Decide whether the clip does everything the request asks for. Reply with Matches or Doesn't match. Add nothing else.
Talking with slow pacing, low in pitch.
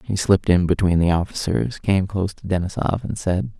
Doesn't match